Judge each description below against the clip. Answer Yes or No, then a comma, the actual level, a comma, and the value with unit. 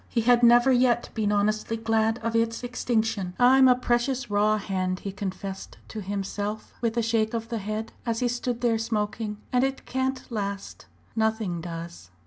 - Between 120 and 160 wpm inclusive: No, average, 175 wpm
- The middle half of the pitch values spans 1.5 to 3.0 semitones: Yes, average, 2.7 semitones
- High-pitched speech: Yes, high, 225 Hz